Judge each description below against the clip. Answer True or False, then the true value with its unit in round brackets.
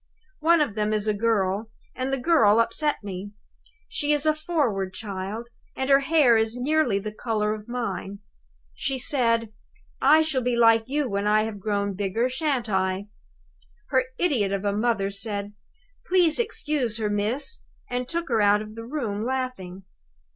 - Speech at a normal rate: True (170 wpm)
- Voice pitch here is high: True (230 Hz)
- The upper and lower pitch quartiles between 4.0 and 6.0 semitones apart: True (4.8 semitones)